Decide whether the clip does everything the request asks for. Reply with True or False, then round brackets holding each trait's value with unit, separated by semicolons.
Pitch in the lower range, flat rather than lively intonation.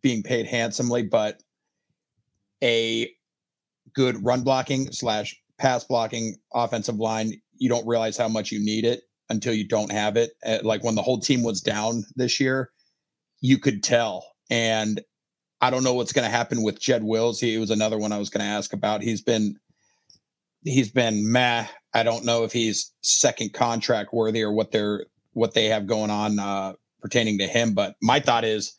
True (115 Hz; 2.1 semitones)